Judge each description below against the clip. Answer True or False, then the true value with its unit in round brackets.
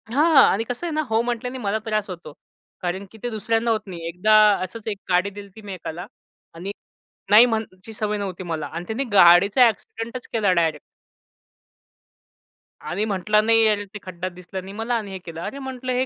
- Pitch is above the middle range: True (205 Hz)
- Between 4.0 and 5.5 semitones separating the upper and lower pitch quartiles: False (3.6 semitones)